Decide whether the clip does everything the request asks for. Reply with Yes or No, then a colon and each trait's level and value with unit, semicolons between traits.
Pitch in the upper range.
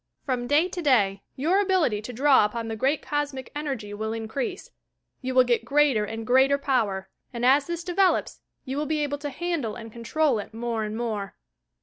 Yes: very high, 255 Hz